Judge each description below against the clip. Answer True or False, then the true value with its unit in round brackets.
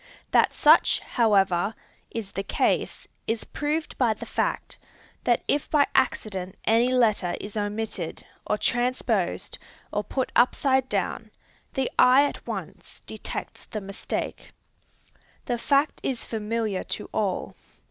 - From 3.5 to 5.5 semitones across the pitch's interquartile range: True (4.1 semitones)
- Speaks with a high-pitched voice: True (225 Hz)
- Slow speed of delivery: True (125 wpm)